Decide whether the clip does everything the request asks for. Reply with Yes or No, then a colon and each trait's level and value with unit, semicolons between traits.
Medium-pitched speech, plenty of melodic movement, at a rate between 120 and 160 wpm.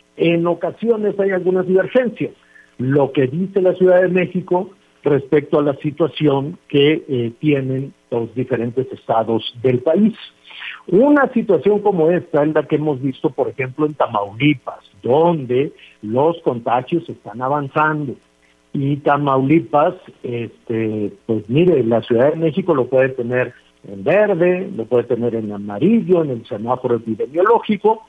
Yes: medium, 145 Hz; wide, 6.6 semitones; average, 140 wpm